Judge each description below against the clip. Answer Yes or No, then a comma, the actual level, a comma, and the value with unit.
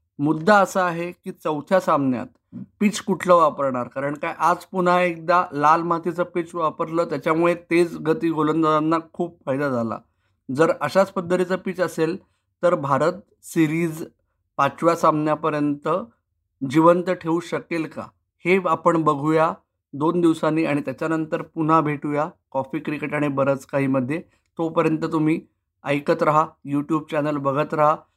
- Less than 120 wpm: No, fast, 130 wpm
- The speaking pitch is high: No, medium, 160 Hz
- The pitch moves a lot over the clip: No, average, 2.9 semitones